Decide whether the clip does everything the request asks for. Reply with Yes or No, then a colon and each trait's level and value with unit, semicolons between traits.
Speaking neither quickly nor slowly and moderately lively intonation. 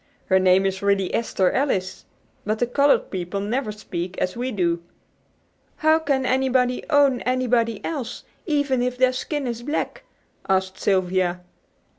No: average, 145 wpm; wide, 5.7 semitones